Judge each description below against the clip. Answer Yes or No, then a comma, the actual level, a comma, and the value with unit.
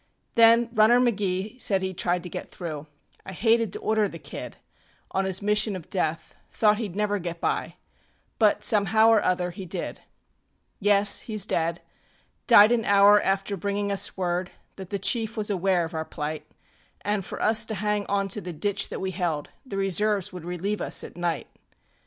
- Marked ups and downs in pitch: No, average, 3.0 semitones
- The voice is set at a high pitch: Yes, high, 200 Hz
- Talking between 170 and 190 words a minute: Yes, average, 180 wpm